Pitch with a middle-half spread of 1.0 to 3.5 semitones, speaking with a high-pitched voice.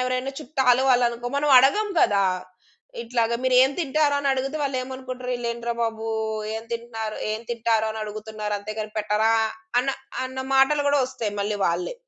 Yes: average, 3.2 semitones; high, 240 Hz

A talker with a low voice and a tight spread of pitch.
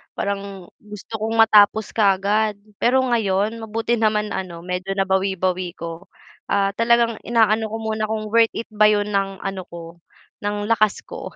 No: high, 210 Hz; narrow, 2.3 semitones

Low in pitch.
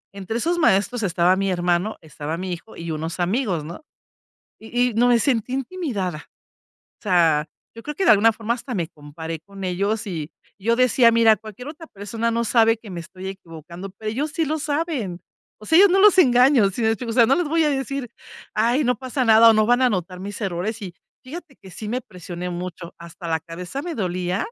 No: high, 215 Hz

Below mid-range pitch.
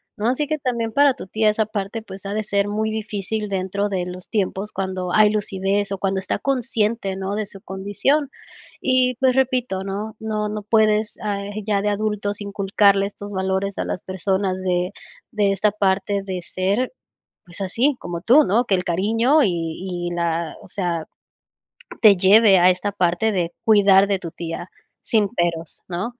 No: high, 200 Hz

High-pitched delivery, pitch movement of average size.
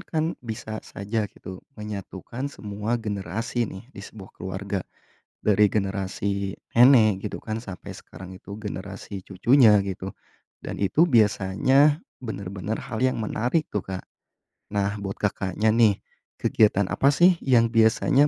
No: low, 105 Hz; average, 3.0 semitones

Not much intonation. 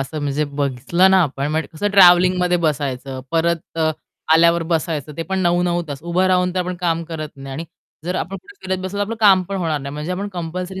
No: average, 3.3 semitones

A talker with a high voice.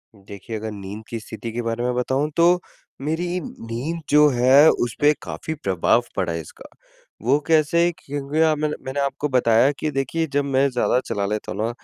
No: low, 130 Hz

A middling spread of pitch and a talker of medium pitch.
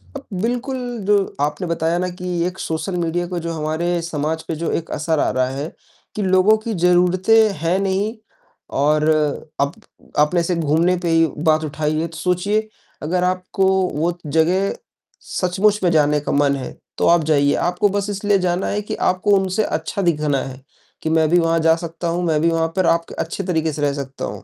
Yes: average, 3.0 semitones; medium, 170 Hz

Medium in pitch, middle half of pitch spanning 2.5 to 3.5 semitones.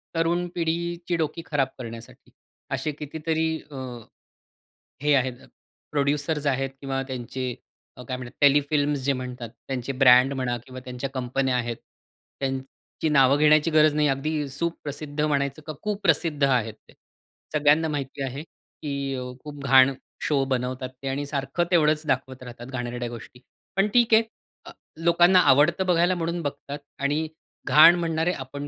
Yes: medium, 145 Hz; average, 3.2 semitones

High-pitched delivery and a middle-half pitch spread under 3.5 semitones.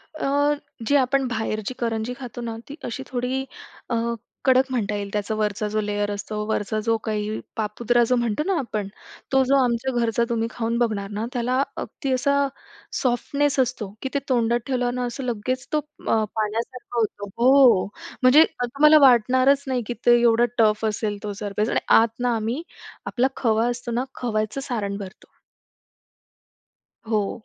Yes: high, 235 Hz; average, 3.0 semitones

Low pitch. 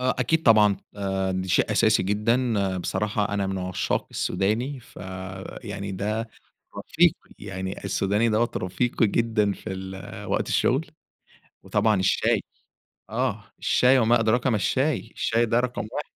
Yes: low, 105 Hz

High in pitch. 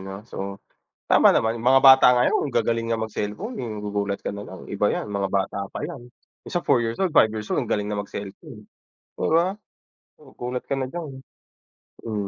No: low, 115 Hz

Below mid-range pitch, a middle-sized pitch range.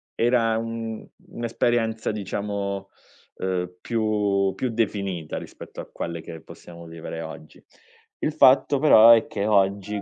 Yes: low, 105 Hz; average, 3.4 semitones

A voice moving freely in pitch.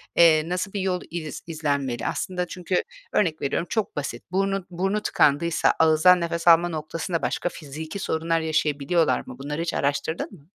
No: average, 2.7 semitones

